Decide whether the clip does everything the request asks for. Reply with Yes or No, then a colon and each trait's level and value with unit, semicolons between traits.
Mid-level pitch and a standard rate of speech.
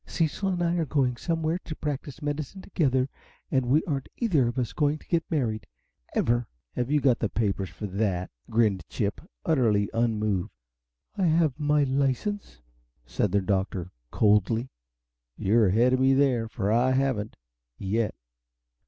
No: low, 125 Hz; average, 160 wpm